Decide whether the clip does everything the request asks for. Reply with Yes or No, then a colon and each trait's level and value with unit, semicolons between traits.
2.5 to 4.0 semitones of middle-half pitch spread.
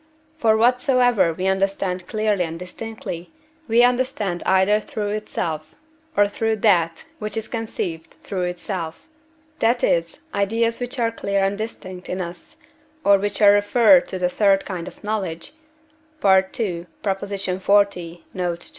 Yes: average, 3.4 semitones